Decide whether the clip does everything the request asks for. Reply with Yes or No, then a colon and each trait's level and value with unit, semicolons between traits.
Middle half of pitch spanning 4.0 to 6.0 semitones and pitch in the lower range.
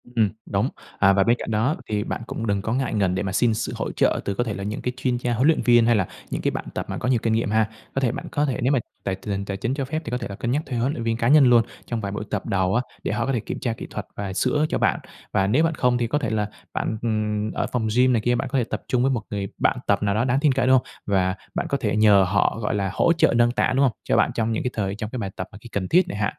No: average, 3.5 semitones; low, 115 Hz